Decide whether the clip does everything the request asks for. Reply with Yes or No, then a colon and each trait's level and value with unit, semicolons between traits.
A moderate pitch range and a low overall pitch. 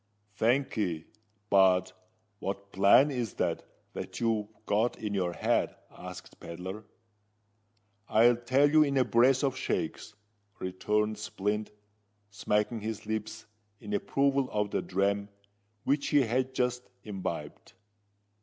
Yes: average, 4.4 semitones; low, 110 Hz